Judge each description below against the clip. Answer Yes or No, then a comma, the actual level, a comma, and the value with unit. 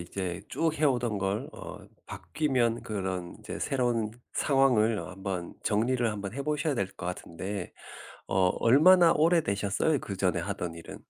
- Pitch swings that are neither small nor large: No, wide, 6.2 semitones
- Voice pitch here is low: Yes, low, 110 Hz